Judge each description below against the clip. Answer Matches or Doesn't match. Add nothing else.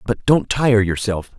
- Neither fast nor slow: Matches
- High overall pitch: Doesn't match